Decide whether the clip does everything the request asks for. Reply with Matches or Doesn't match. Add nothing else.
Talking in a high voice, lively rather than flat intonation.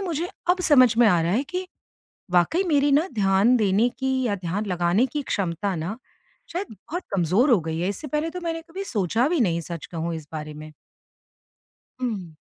Matches